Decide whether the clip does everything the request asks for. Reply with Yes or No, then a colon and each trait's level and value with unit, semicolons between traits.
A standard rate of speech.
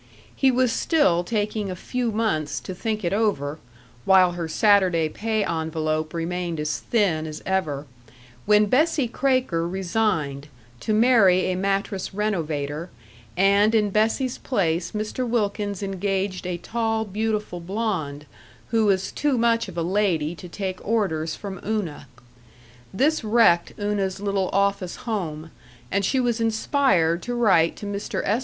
Yes: average, 145 wpm